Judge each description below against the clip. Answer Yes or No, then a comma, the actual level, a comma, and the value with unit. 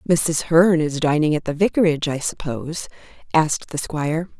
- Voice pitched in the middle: Yes, medium, 155 Hz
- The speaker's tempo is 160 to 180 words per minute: Yes, average, 165 wpm